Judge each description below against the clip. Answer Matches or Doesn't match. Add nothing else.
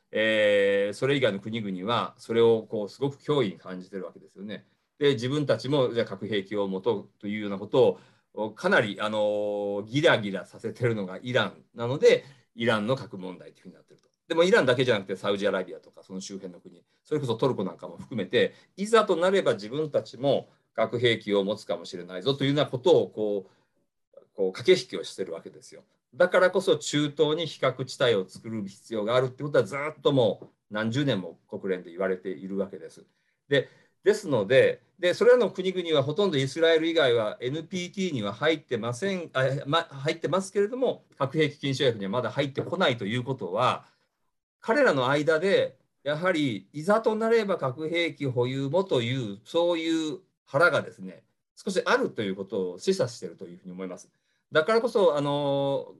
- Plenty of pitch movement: Matches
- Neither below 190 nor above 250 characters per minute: Doesn't match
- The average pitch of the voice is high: Doesn't match